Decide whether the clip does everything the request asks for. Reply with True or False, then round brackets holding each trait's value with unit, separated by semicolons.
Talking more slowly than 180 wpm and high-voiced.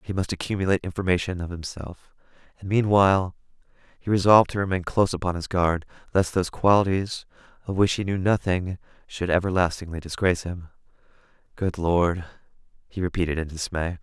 False (145 wpm; 90 Hz)